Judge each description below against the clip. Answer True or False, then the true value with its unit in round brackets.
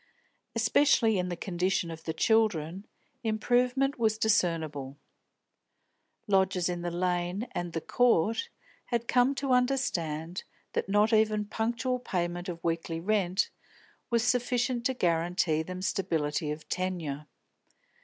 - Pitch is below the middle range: False (190 Hz)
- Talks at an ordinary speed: False (125 wpm)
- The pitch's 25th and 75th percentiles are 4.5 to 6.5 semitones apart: True (5.4 semitones)